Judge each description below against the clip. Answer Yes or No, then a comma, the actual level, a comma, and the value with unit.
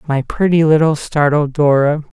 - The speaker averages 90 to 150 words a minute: Yes, slow, 135 wpm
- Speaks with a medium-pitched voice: Yes, medium, 150 Hz